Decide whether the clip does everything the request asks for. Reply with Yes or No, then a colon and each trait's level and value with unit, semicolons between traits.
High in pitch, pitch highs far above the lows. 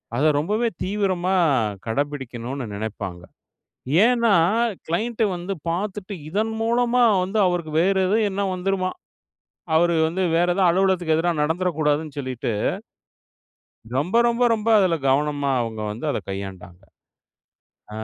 No: medium, 175 Hz; wide, 5.9 semitones